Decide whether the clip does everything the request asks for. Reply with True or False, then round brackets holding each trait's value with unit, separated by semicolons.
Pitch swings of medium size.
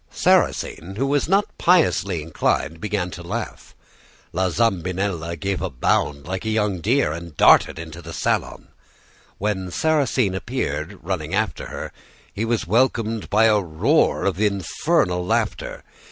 True (4.7 semitones)